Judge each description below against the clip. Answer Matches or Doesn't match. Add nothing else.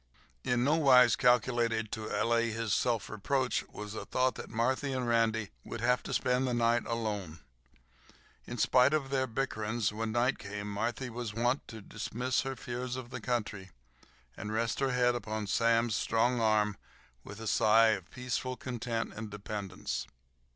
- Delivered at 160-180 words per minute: Matches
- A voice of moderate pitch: Doesn't match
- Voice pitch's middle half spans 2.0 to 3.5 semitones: Matches